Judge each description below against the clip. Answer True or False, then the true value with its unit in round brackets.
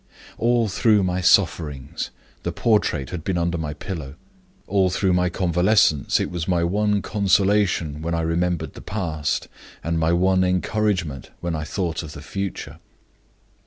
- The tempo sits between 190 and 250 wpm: False (155 wpm)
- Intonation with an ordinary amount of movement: True (3.4 semitones)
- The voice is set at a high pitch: False (90 Hz)